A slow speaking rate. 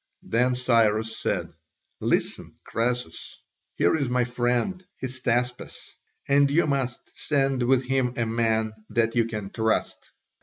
Yes: slow, 125 wpm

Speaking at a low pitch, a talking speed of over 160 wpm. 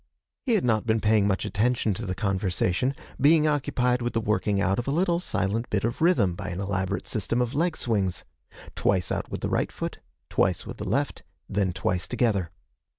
Yes: low, 110 Hz; average, 200 wpm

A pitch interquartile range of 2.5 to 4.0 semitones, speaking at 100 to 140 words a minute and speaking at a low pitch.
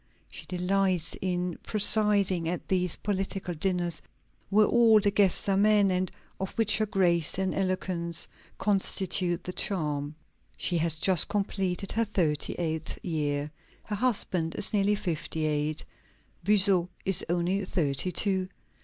No: average, 2.9 semitones; slow, 135 wpm; medium, 185 Hz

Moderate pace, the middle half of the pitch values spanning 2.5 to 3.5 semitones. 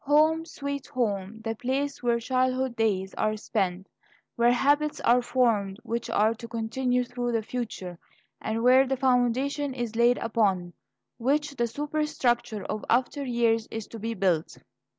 Yes: average, 150 wpm; average, 2.9 semitones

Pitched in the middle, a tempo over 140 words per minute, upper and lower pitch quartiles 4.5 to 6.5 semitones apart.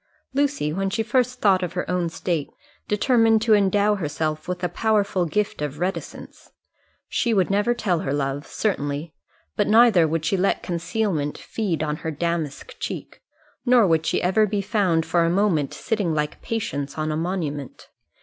Yes: medium, 180 Hz; average, 170 wpm; average, 5.1 semitones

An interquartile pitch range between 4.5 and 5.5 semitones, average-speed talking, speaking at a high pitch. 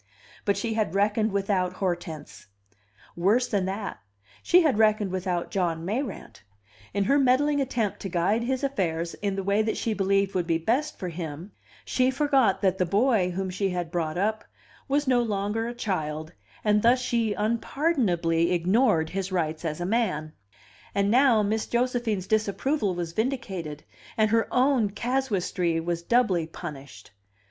Yes: average, 5.0 semitones; average, 160 wpm; high, 200 Hz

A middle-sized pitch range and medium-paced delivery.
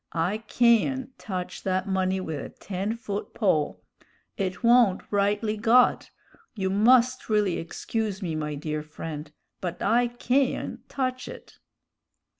No: average, 4.3 semitones; slow, 130 wpm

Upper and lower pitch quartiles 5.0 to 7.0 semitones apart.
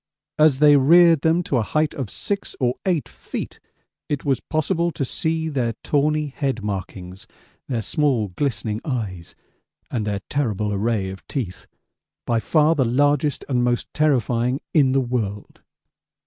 Yes: wide, 5.4 semitones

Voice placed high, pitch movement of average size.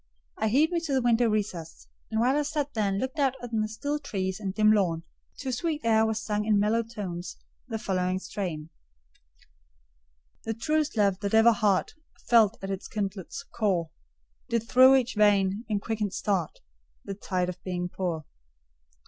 Yes: high, 215 Hz; average, 3.7 semitones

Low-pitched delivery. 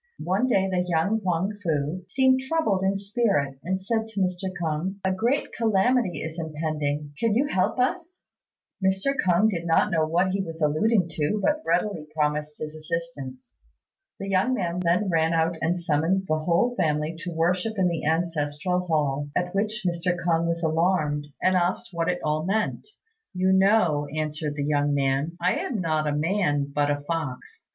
No: medium, 175 Hz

